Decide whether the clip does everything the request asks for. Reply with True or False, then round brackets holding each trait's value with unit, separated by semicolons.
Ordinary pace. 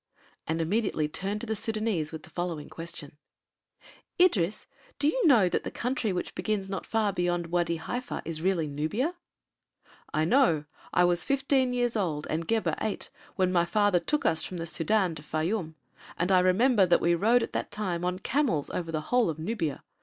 True (190 wpm)